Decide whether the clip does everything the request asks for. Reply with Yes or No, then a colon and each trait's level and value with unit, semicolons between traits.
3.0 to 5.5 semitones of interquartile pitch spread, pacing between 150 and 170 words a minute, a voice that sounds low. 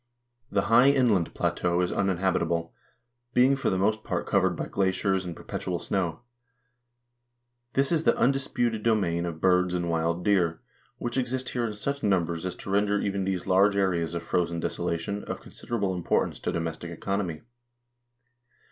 Yes: average, 3.7 semitones; average, 165 wpm; very low, 95 Hz